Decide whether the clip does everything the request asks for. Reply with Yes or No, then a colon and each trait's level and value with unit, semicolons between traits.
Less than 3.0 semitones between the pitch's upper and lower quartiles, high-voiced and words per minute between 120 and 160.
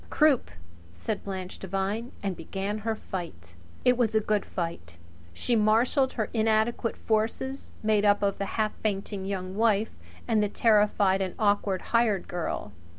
Yes: narrow, 2.6 semitones; high, 210 Hz; average, 155 wpm